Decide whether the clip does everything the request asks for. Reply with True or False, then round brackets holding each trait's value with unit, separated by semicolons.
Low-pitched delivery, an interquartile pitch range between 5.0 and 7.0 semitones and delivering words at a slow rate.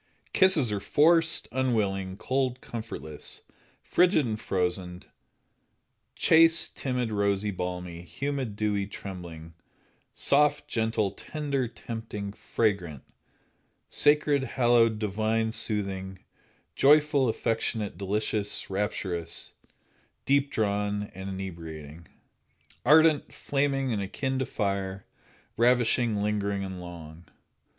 True (105 Hz; 5.3 semitones; 95 wpm)